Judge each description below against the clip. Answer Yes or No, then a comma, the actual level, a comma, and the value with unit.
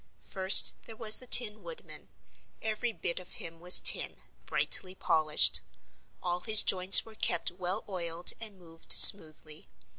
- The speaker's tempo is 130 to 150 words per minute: Yes, average, 145 wpm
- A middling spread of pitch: Yes, average, 4.1 semitones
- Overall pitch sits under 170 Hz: No, medium, 185 Hz